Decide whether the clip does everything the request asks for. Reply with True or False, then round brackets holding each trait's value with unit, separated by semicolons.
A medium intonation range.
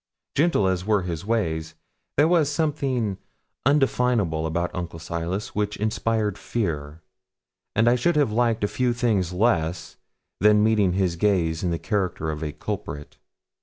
False (5.8 semitones)